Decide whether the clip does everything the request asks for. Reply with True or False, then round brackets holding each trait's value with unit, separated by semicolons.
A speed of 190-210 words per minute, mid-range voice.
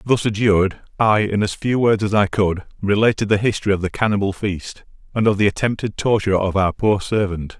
False (205 wpm; 100 Hz)